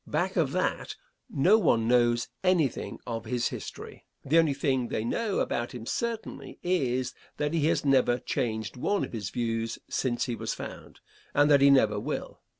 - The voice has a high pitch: No, low, 125 Hz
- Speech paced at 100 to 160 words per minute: No, average, 175 wpm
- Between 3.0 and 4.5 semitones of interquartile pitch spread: Yes, average, 3.9 semitones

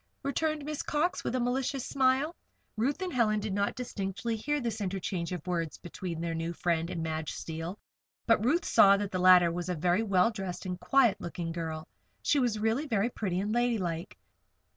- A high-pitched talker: Yes, high, 200 Hz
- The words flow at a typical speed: Yes, average, 195 wpm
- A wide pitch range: Yes, wide, 5.9 semitones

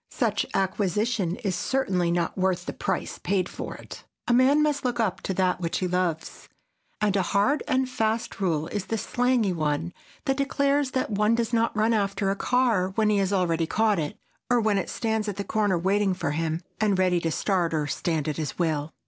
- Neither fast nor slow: No, fast, 210 wpm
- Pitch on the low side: No, high, 200 Hz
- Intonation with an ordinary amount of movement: Yes, average, 4.4 semitones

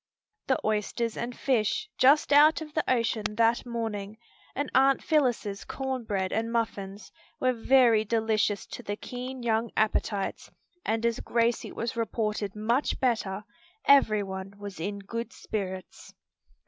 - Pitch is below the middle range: No, high, 225 Hz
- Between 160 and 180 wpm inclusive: No, average, 140 wpm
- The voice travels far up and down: No, average, 3.3 semitones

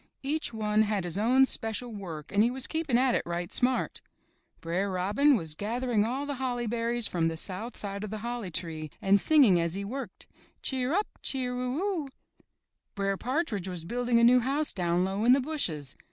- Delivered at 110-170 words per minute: No, average, 195 wpm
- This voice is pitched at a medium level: No, high, 225 Hz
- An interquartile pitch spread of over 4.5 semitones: Yes, average, 5.3 semitones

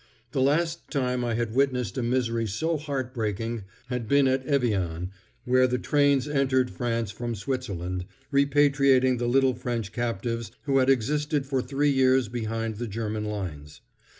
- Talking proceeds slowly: No, average, 155 wpm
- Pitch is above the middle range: No, low, 125 Hz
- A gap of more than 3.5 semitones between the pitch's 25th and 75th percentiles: No, average, 3.2 semitones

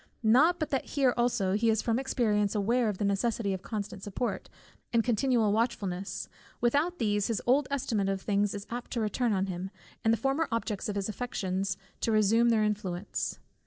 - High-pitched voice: Yes, high, 220 Hz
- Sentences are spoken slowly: No, average, 190 wpm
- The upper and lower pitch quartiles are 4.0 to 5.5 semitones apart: No, average, 3.2 semitones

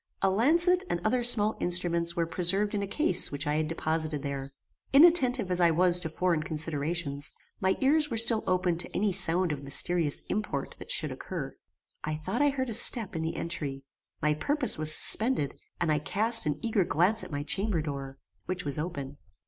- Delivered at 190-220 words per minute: Yes, average, 195 wpm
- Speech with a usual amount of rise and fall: No, wide, 6.0 semitones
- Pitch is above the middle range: No, medium, 175 Hz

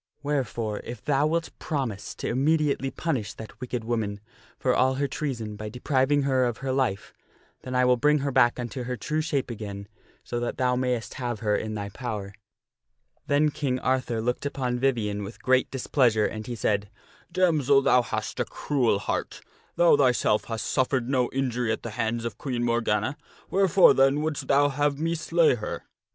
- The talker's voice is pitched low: Yes, low, 125 Hz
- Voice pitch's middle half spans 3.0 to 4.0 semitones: Yes, average, 3.7 semitones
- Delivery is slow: No, average, 185 wpm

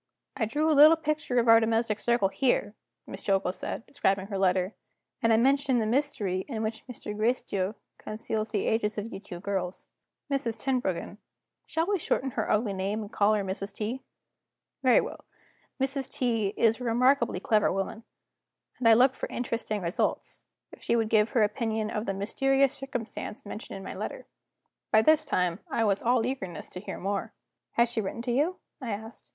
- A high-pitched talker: Yes, high, 225 Hz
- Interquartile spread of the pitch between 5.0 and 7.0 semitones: No, average, 3.7 semitones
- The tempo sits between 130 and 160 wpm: No, average, 190 wpm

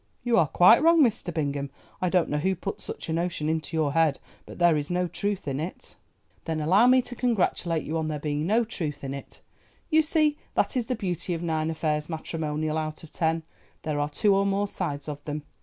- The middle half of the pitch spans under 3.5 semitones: No, average, 4.5 semitones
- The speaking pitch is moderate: Yes, medium, 165 Hz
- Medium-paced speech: No, fast, 220 wpm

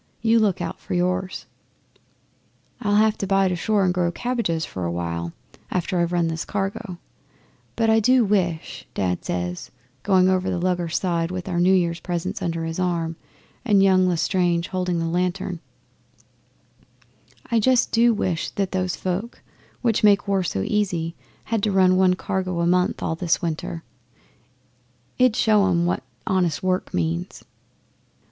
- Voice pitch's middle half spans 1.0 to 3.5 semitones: Yes, narrow, 2.6 semitones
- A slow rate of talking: No, average, 160 wpm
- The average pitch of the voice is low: No, medium, 180 Hz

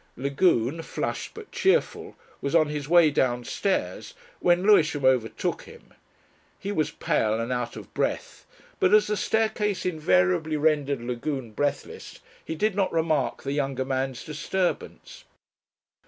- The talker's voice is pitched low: No, medium, 150 Hz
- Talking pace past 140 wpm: No, slow, 135 wpm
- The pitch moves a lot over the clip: Yes, wide, 5.7 semitones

